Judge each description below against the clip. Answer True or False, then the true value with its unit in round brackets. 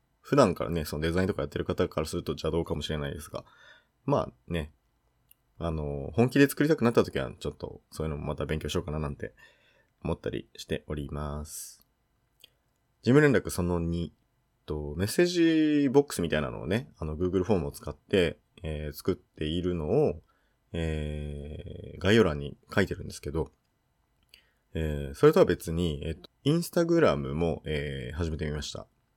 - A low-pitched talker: True (80 Hz)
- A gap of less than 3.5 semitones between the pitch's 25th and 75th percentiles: False (4.4 semitones)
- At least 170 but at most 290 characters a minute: False (360 characters per minute)